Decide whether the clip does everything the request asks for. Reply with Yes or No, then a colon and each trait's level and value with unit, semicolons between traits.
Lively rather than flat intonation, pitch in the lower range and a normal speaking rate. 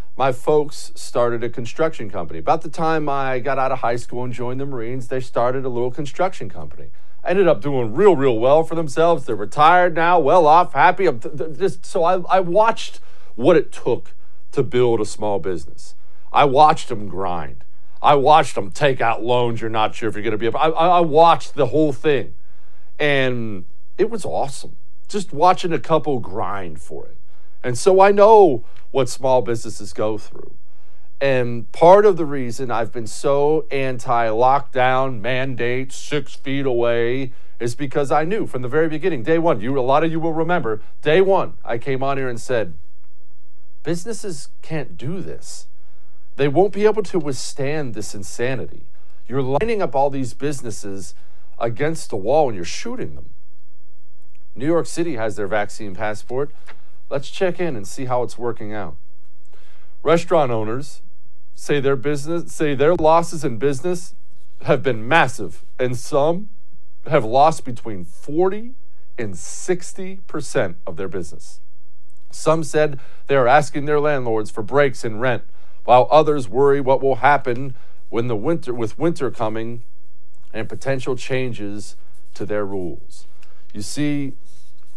Yes: wide, 6.2 semitones; low, 130 Hz; average, 165 wpm